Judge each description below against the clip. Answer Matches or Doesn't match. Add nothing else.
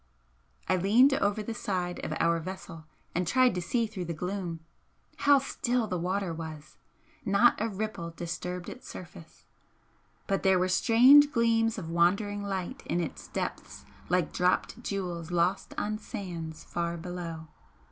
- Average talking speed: Matches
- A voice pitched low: Doesn't match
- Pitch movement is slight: Doesn't match